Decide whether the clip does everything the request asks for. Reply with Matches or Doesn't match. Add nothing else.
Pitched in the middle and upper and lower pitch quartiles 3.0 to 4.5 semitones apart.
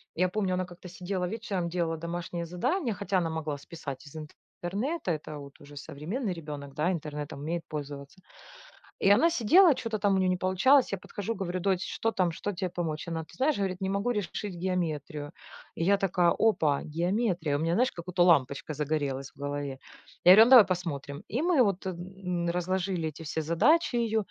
Matches